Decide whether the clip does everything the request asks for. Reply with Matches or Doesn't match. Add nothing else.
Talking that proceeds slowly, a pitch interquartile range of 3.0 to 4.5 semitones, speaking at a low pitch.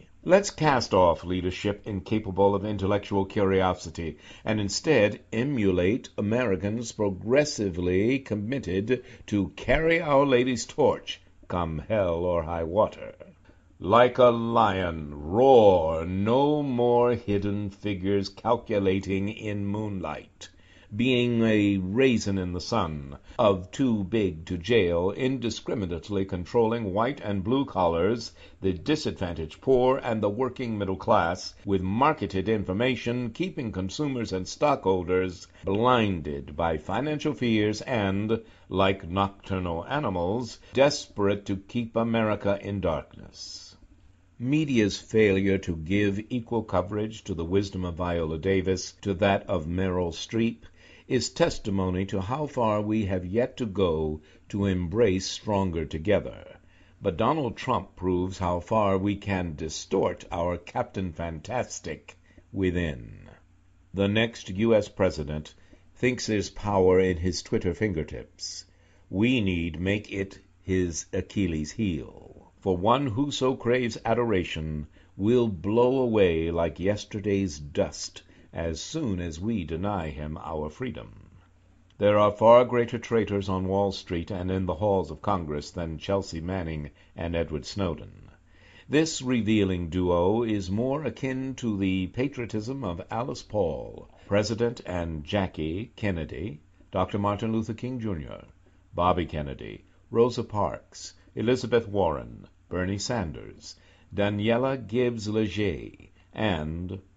Matches